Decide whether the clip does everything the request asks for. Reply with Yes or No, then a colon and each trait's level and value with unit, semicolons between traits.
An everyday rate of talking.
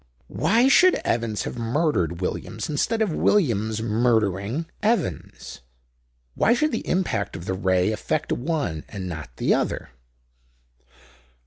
No: slow, 125 wpm